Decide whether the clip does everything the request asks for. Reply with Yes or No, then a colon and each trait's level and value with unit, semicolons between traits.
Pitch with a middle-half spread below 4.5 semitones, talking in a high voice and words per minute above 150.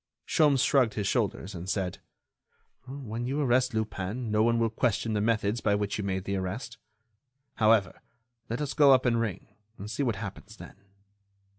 No: average, 3.6 semitones; low, 110 Hz; average, 175 wpm